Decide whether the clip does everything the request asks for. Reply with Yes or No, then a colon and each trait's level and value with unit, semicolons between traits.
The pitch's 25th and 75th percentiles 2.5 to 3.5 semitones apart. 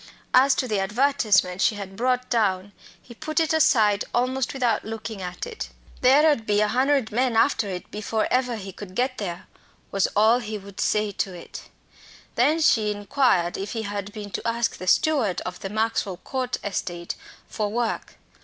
No: average, 4.1 semitones